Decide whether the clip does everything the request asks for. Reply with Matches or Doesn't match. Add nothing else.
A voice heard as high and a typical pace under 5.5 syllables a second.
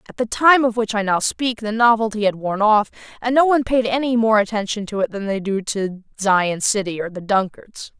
Matches